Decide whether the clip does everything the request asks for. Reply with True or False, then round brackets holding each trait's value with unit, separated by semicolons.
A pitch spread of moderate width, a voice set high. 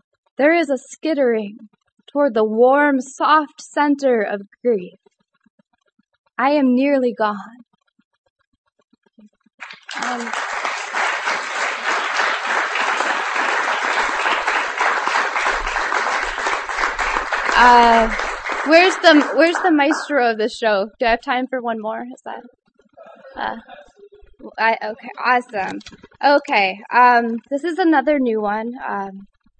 True (4.4 semitones; 240 Hz)